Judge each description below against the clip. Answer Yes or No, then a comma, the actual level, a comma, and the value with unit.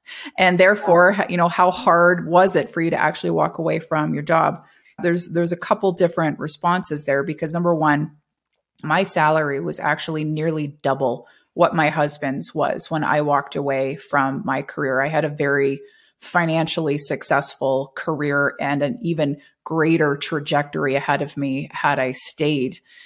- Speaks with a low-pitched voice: No, medium, 155 Hz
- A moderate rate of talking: Yes, average, 160 wpm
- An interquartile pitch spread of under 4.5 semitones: Yes, average, 3.3 semitones